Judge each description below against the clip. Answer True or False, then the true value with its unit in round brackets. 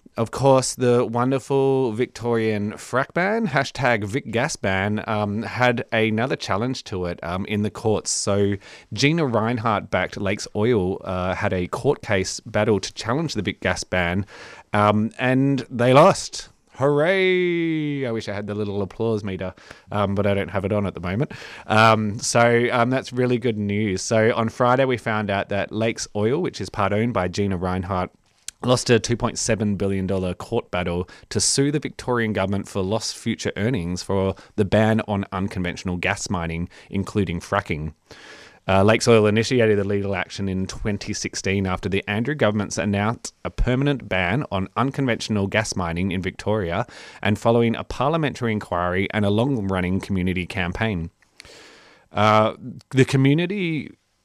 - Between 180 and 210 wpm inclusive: False (160 wpm)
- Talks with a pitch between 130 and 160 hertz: False (105 Hz)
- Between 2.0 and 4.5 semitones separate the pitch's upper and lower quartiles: True (3.8 semitones)